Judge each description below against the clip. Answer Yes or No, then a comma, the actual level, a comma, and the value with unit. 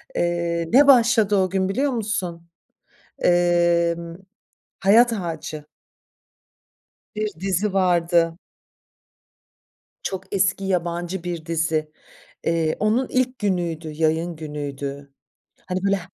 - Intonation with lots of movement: No, average, 2.8 semitones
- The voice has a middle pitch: Yes, medium, 175 Hz